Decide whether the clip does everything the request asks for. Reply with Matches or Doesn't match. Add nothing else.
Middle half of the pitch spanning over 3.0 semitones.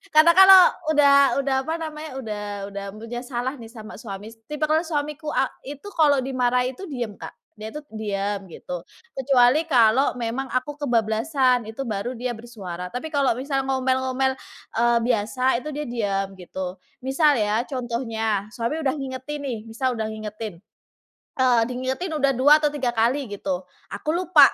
Matches